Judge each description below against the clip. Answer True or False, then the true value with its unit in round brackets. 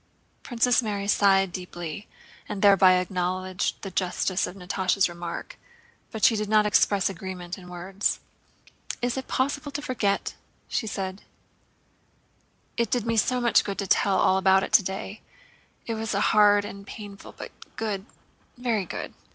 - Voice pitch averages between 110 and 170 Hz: False (200 Hz)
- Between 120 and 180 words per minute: True (150 wpm)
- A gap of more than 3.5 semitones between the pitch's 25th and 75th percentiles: False (2.6 semitones)